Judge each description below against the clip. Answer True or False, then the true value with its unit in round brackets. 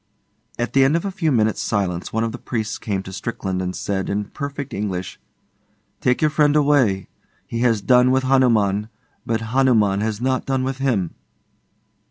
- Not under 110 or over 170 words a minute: False (180 wpm)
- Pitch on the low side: True (115 Hz)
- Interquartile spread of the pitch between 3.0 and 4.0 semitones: False (4.6 semitones)